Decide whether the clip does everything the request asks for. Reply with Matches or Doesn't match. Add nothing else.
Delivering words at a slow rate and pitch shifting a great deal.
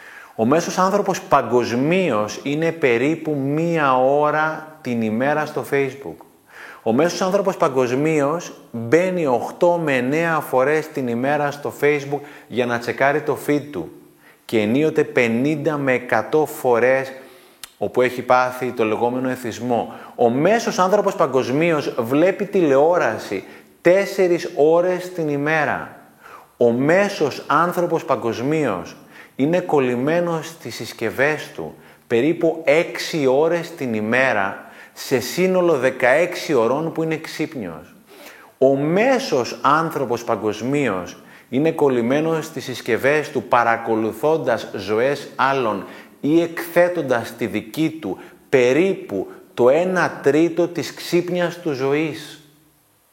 Doesn't match